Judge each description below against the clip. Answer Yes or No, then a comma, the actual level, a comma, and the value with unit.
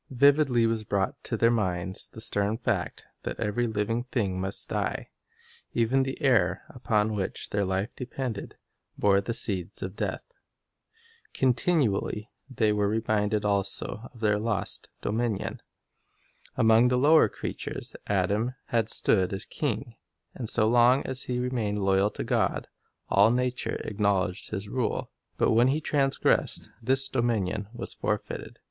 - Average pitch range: Yes, average, 3.5 semitones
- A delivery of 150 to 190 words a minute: No, average, 140 wpm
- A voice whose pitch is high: No, low, 110 Hz